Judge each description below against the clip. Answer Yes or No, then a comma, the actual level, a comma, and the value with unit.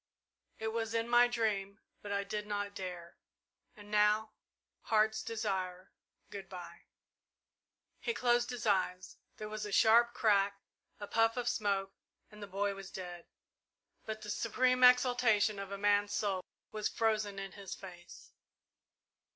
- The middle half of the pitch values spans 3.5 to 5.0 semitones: No, narrow, 2.4 semitones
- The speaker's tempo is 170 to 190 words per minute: No, average, 145 wpm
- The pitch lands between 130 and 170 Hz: No, high, 210 Hz